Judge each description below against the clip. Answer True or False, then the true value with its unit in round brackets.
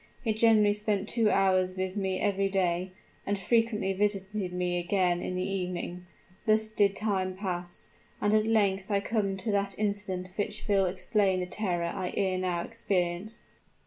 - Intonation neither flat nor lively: False (2.2 semitones)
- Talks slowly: False (165 wpm)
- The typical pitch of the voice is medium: False (195 Hz)